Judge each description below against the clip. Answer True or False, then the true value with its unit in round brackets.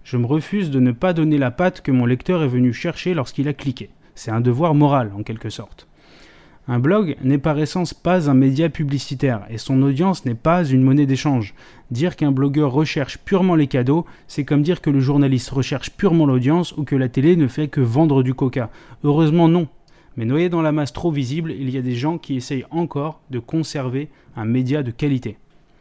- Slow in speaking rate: False (210 wpm)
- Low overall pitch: False (145 Hz)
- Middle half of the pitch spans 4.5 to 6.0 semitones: False (3.7 semitones)